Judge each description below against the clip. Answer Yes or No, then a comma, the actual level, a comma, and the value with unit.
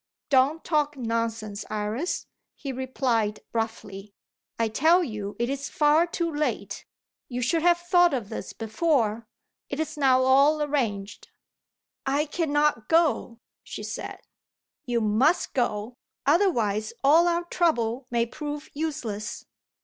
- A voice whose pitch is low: No, very high, 265 Hz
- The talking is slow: Yes, slow, 125 wpm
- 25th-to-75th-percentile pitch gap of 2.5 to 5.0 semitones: No, wide, 5.5 semitones